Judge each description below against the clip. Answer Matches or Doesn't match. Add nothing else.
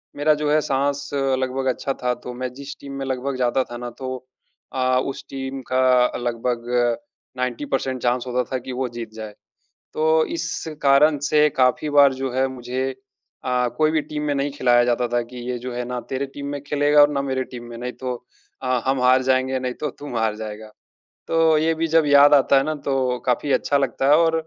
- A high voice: Doesn't match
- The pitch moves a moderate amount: Doesn't match